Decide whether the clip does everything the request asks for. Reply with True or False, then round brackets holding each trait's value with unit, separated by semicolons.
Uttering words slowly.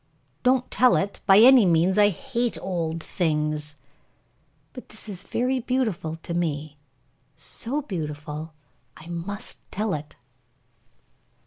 True (120 wpm)